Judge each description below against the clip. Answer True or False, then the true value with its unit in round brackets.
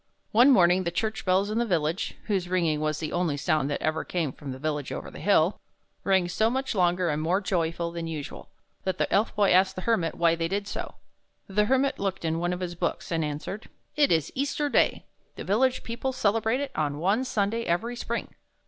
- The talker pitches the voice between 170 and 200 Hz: True (185 Hz)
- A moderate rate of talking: False (220 wpm)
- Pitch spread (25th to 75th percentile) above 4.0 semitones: True (5.0 semitones)